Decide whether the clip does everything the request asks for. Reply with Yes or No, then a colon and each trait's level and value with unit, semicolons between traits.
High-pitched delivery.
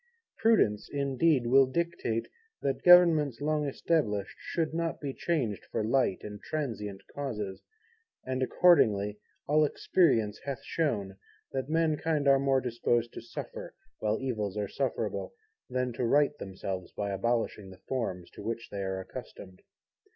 No: low, 130 Hz